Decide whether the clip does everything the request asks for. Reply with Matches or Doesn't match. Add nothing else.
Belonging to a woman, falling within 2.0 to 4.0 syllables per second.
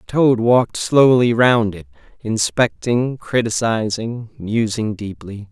Doesn't match